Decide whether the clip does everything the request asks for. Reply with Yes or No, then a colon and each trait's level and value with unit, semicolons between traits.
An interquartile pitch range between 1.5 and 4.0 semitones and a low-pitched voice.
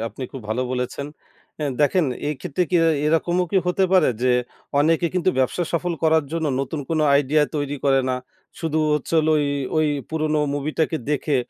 No: average, 2.7 semitones; medium, 155 Hz